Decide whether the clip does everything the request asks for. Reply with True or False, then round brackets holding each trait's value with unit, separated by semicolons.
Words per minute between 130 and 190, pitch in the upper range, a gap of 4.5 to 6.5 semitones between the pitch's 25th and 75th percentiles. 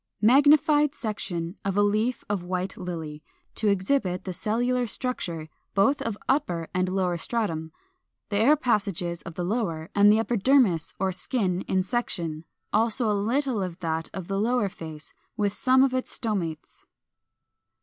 True (155 wpm; 200 Hz; 5.3 semitones)